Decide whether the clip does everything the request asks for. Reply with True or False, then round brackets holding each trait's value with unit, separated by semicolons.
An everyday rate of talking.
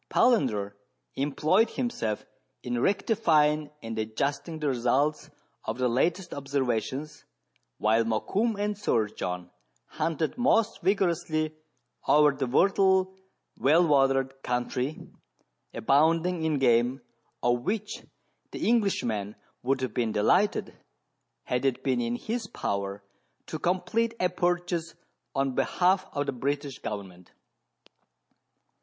False (110 wpm)